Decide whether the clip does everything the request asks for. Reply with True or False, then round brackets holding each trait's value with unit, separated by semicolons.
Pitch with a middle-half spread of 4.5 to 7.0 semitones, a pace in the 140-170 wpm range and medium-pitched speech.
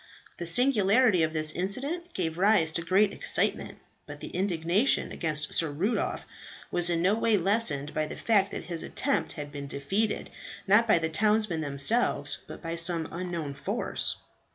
True (4.9 semitones; 165 wpm; 175 Hz)